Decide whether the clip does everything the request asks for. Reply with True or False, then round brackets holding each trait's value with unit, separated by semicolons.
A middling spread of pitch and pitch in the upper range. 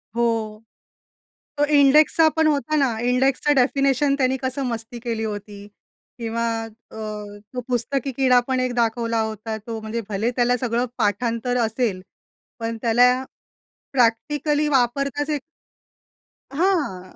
True (3.4 semitones; 245 Hz)